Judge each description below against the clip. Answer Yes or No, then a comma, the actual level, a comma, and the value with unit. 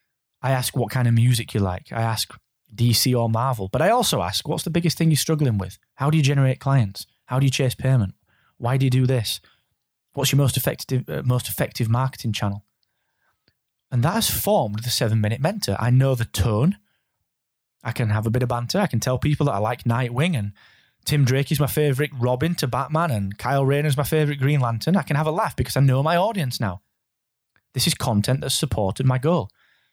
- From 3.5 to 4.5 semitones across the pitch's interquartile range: Yes, average, 3.9 semitones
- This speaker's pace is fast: Yes, fast, 220 wpm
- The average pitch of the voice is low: Yes, low, 130 Hz